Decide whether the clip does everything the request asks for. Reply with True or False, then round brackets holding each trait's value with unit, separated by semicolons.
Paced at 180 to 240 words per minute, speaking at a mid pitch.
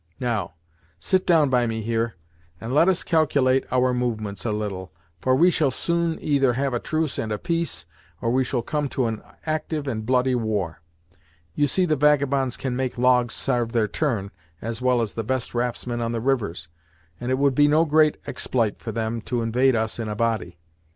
False (200 wpm; 125 Hz)